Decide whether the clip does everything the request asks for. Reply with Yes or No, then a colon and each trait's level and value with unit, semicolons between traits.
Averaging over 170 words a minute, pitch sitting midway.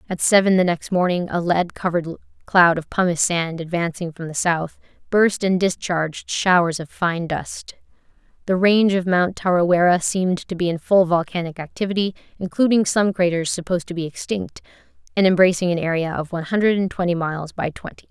Yes: average, 180 wpm; medium, 175 Hz